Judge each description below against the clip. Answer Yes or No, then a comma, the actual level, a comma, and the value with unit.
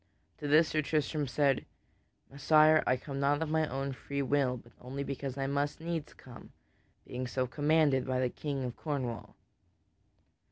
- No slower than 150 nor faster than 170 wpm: Yes, average, 165 wpm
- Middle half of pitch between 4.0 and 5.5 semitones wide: No, average, 2.7 semitones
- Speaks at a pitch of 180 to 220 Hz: No, medium, 140 Hz